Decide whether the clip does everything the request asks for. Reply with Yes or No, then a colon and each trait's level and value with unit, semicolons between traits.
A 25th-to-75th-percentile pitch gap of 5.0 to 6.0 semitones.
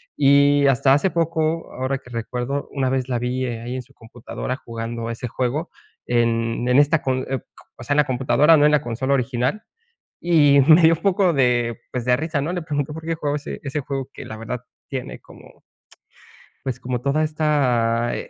No: average, 3.4 semitones